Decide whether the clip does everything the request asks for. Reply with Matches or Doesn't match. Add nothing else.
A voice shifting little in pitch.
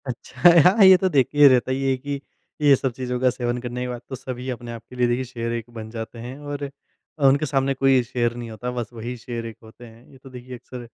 Matches